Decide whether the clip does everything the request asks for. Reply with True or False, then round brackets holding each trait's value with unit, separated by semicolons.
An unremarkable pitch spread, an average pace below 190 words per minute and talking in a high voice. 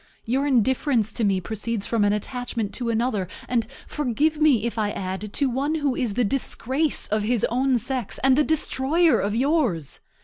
True (4.2 semitones; 180 wpm; 245 Hz)